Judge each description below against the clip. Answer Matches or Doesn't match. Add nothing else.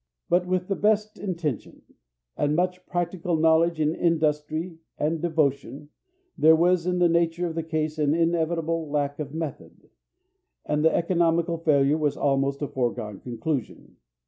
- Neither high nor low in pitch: Matches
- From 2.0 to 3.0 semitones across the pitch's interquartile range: Matches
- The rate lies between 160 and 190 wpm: Doesn't match